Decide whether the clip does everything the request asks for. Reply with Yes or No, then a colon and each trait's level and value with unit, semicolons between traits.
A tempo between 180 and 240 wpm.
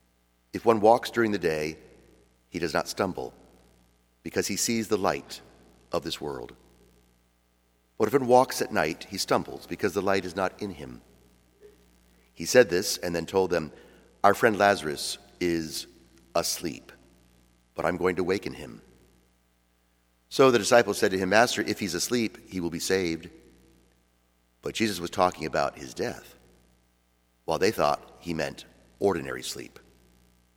No: average, 155 wpm